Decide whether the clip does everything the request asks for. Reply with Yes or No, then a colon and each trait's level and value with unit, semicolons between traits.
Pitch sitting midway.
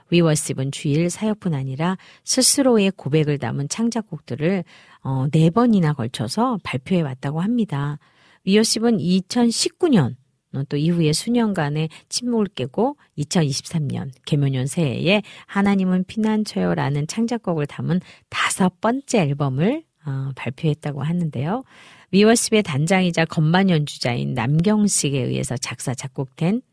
Yes: medium, 165 Hz